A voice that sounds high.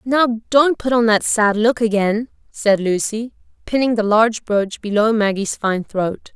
Yes: high, 220 Hz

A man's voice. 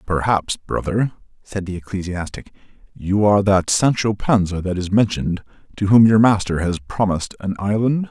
Yes: male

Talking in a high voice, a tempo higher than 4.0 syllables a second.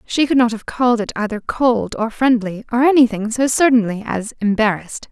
Yes: high, 230 Hz; 5.5 syllables/s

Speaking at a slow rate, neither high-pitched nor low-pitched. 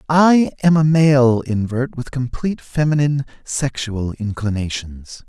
No: slow, 115 wpm; low, 130 Hz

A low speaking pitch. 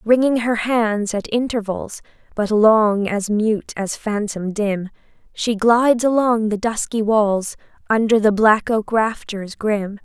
No: high, 215 Hz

